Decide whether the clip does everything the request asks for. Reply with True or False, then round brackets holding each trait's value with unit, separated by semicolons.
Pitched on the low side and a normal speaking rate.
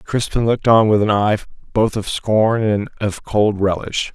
True (105 Hz; 190 wpm)